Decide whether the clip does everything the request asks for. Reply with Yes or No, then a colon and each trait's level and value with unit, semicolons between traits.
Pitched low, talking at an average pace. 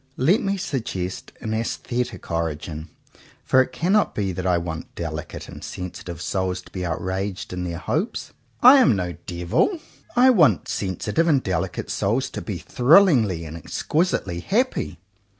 Yes: very low, 95 Hz; average, 155 wpm